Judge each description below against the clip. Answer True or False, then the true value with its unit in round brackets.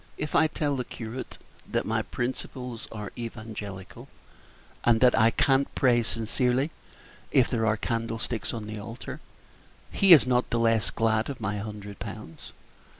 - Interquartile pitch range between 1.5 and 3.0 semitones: True (2.7 semitones)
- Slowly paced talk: False (160 wpm)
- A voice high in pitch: False (115 Hz)